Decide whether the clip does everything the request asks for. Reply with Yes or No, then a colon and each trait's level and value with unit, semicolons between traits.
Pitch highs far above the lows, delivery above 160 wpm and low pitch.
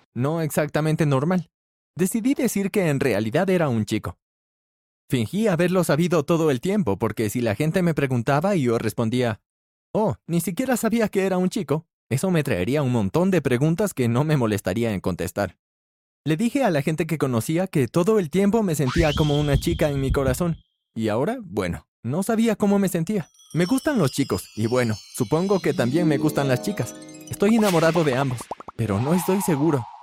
No: wide, 7.1 semitones; fast, 190 wpm; medium, 155 Hz